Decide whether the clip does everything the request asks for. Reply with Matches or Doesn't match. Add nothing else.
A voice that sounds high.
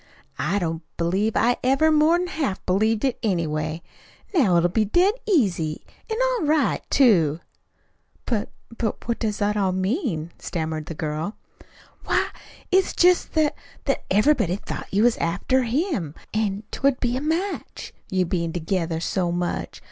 Matches